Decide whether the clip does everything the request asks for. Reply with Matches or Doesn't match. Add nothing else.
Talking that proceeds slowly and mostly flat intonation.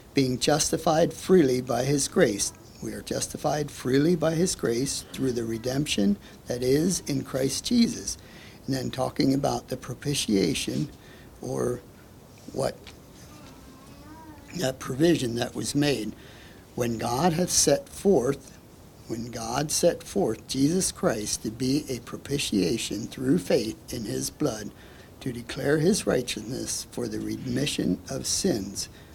Doesn't match